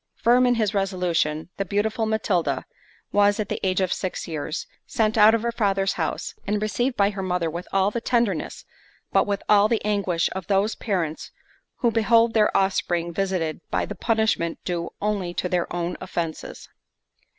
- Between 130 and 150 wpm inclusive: No, average, 175 wpm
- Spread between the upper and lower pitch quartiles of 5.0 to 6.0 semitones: No, average, 3.5 semitones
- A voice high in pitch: Yes, high, 195 Hz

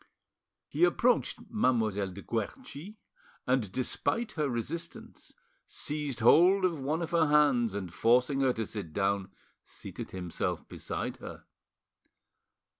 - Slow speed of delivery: Yes, slow, 120 wpm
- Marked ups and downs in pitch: Yes, wide, 7.4 semitones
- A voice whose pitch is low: Yes, low, 130 Hz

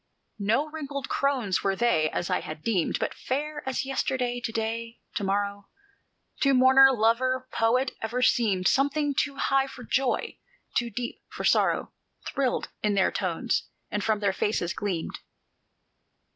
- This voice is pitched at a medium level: No, high, 235 Hz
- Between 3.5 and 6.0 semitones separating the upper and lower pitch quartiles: Yes, average, 4.7 semitones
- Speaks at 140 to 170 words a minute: Yes, average, 150 wpm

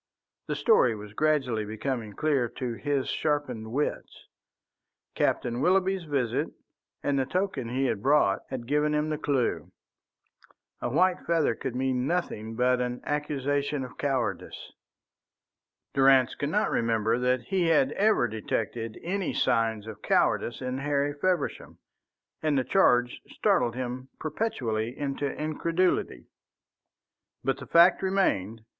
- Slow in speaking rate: Yes, slow, 130 wpm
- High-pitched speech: No, low, 135 Hz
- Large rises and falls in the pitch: No, average, 4.1 semitones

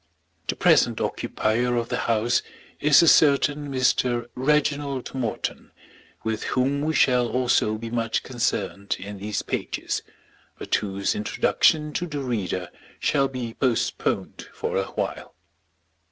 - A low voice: Yes, low, 125 Hz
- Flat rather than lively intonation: No, average, 4.0 semitones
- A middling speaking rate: No, slow, 125 wpm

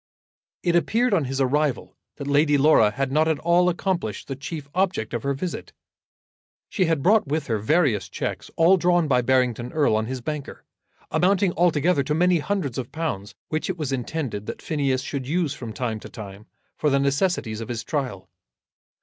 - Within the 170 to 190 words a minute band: Yes, average, 185 wpm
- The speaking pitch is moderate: Yes, medium, 145 Hz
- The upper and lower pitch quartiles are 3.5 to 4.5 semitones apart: No, average, 5.3 semitones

